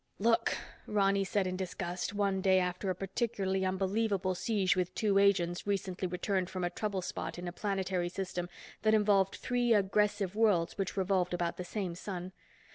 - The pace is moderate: Yes, average, 170 wpm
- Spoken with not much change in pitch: Yes, narrow, 2.0 semitones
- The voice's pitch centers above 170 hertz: Yes, high, 190 Hz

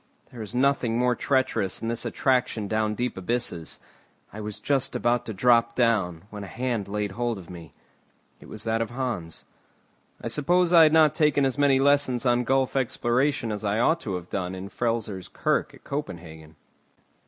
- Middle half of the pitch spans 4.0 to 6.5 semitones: Yes, average, 4.4 semitones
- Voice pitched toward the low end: Yes, low, 115 Hz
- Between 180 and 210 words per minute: Yes, average, 190 wpm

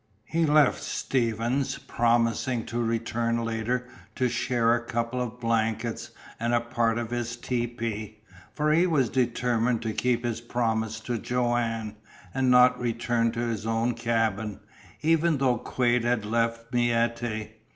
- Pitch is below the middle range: Yes, low, 120 Hz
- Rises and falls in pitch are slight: Yes, narrow, 1.4 semitones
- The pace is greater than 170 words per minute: No, average, 140 wpm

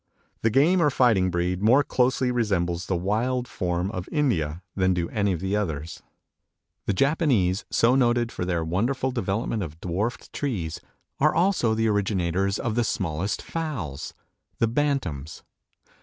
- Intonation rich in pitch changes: Yes, wide, 5.9 semitones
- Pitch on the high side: No, low, 105 Hz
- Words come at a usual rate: Yes, average, 150 wpm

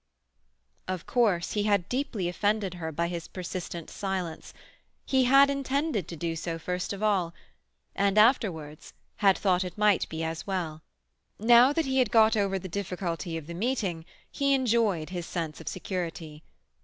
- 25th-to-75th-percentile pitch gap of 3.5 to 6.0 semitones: Yes, average, 4.4 semitones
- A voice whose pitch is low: No, high, 190 Hz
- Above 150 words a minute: Yes, average, 160 wpm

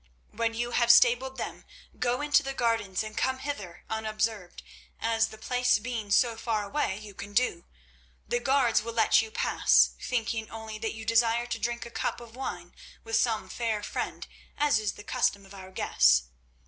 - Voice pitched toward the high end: Yes, high, 225 Hz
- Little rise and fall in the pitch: Yes, narrow, 2.2 semitones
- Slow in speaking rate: No, average, 185 wpm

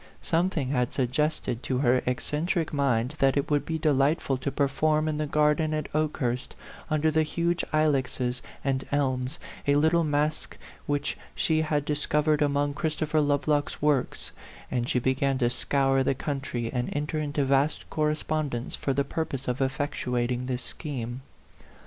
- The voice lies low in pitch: No, medium, 145 Hz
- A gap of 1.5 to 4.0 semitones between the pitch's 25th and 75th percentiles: Yes, average, 2.7 semitones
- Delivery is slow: No, average, 160 wpm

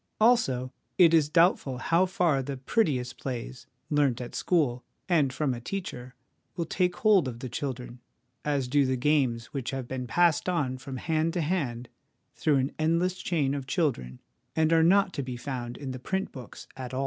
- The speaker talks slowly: No, average, 185 wpm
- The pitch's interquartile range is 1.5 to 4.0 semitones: No, average, 4.7 semitones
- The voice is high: No, medium, 140 Hz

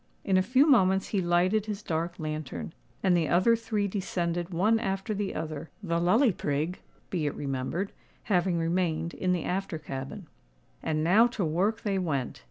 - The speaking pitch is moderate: Yes, medium, 180 Hz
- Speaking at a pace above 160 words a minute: Yes, average, 175 wpm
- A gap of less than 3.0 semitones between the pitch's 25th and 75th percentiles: No, average, 3.7 semitones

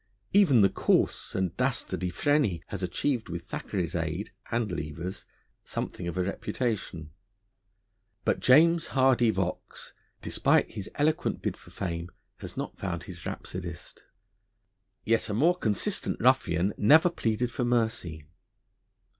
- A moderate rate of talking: No, slow, 130 wpm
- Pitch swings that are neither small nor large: No, wide, 6.1 semitones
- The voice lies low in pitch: Yes, low, 100 Hz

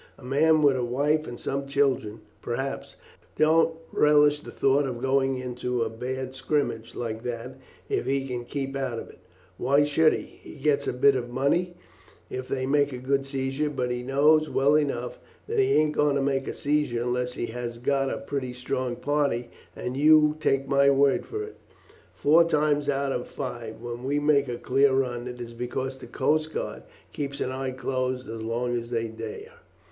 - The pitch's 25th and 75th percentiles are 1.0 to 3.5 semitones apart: Yes, average, 2.8 semitones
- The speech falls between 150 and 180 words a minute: No, average, 195 wpm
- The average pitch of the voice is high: No, low, 135 Hz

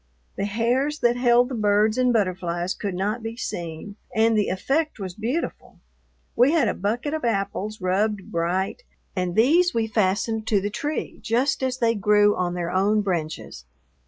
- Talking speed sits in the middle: Yes, average, 170 wpm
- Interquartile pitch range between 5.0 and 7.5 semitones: No, average, 4.1 semitones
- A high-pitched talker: Yes, high, 215 Hz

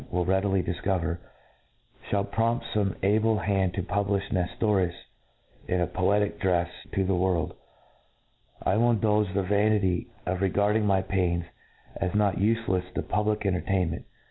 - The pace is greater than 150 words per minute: No, average, 145 wpm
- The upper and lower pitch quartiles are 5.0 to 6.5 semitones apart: No, narrow, 2.4 semitones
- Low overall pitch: Yes, very low, 95 Hz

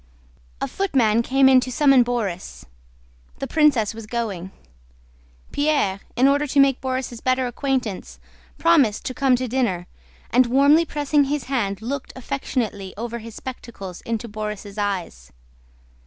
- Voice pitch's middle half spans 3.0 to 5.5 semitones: Yes, average, 4.7 semitones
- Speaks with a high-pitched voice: Yes, high, 245 Hz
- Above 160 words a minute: No, slow, 135 wpm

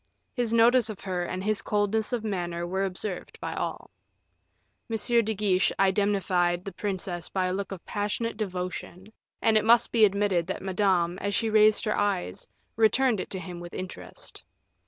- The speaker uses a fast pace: No, average, 175 wpm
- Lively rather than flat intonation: No, average, 2.9 semitones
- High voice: Yes, high, 200 Hz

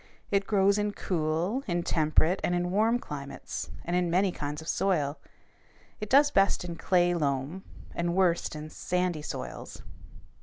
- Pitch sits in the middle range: Yes, medium, 175 Hz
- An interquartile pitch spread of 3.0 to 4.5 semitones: Yes, average, 3.7 semitones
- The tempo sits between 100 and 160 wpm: Yes, average, 155 wpm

